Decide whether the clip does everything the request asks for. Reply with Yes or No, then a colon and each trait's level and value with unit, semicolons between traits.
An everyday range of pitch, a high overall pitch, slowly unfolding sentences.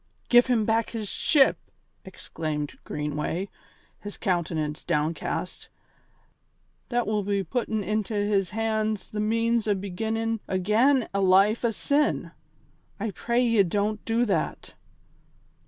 Yes: average, 3.2 semitones; high, 210 Hz; slow, 120 wpm